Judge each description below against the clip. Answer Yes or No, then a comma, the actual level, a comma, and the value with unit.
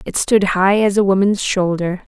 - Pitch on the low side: No, high, 195 Hz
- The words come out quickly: No, average, 195 wpm